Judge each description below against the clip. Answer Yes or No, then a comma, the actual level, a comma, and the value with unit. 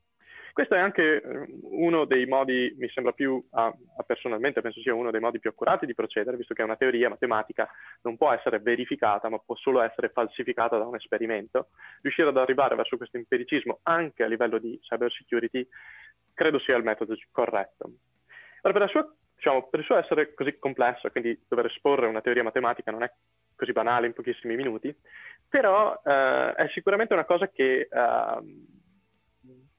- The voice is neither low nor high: No, low, 130 Hz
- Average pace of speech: No, fast, 175 wpm